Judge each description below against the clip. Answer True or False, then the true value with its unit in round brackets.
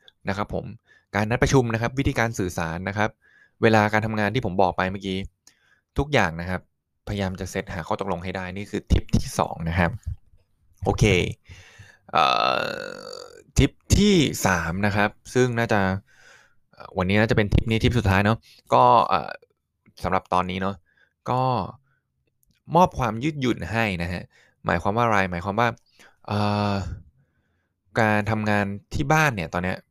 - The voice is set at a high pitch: False (100 Hz)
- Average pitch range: True (3.8 semitones)